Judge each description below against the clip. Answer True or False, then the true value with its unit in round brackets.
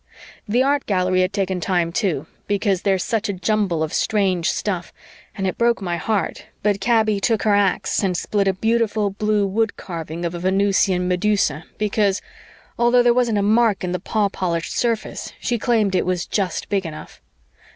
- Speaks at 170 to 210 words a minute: True (180 wpm)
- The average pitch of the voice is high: True (200 Hz)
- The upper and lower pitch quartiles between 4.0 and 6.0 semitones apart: False (2.9 semitones)